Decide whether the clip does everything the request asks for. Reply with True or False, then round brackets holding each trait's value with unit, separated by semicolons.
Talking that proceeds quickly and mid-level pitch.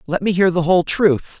True (255 wpm; 180 Hz)